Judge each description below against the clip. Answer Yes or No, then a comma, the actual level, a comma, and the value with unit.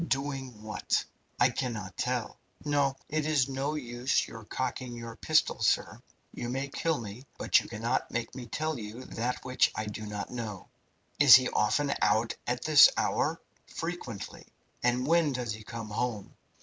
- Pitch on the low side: Yes, low, 125 Hz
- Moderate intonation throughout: Yes, average, 3.4 semitones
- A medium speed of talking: Yes, average, 165 wpm